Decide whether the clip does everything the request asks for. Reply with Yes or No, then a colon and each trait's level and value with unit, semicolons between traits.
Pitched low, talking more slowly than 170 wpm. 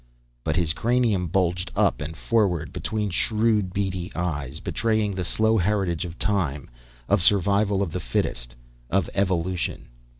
Yes: very low, 95 Hz; average, 140 wpm